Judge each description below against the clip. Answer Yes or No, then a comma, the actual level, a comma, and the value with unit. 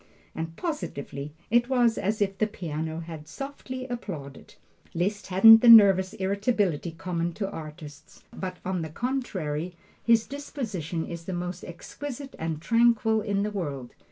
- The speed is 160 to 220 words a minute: No, average, 145 wpm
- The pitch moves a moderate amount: No, wide, 5.9 semitones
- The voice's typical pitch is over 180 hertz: Yes, high, 190 Hz